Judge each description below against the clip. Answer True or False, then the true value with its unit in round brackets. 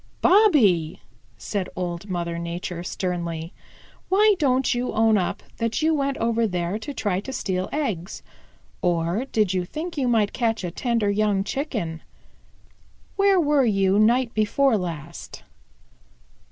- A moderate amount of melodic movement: False (6.6 semitones)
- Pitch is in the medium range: False (210 Hz)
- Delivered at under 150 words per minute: True (140 wpm)